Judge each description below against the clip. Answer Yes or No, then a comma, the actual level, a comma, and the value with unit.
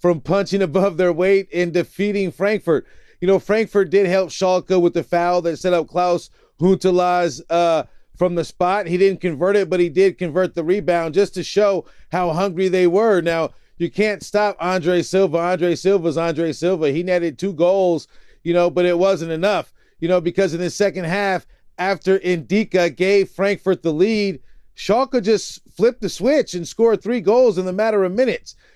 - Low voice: No, medium, 185 Hz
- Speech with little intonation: Yes, narrow, 2.2 semitones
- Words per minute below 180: No, average, 190 wpm